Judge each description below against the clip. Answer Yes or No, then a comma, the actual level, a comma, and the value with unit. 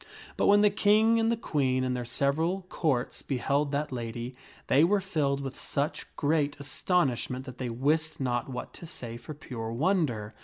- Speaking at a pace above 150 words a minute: Yes, average, 180 wpm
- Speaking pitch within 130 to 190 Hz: Yes, medium, 140 Hz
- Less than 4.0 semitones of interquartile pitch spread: No, average, 4.5 semitones